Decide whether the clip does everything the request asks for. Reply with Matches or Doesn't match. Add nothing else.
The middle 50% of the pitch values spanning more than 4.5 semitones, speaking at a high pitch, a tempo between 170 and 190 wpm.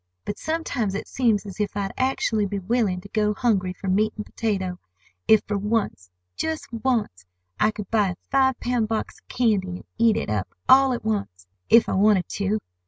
Doesn't match